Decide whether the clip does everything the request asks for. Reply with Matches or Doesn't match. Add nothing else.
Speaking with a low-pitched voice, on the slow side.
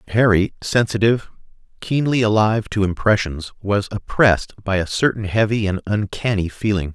Matches